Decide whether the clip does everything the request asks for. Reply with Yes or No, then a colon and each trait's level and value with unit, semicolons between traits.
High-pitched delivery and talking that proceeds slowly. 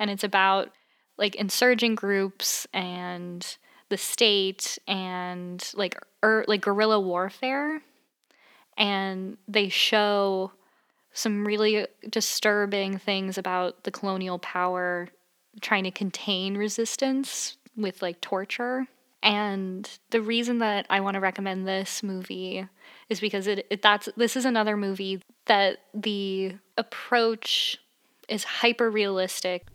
Yes: high, 200 Hz; slow, 115 wpm